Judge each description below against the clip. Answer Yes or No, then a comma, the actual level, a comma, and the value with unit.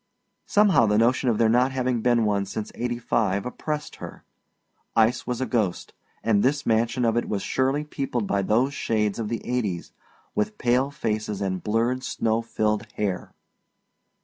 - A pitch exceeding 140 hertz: No, low, 115 Hz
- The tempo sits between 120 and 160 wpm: No, average, 170 wpm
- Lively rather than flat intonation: No, average, 2.9 semitones